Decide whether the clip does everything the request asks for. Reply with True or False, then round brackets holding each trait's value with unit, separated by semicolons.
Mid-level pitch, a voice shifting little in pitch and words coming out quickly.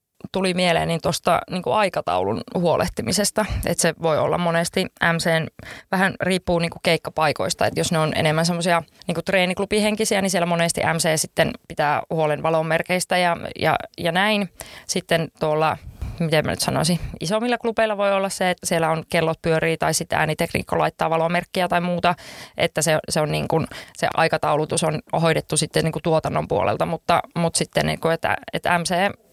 True (170 Hz; 2.3 semitones; 165 wpm)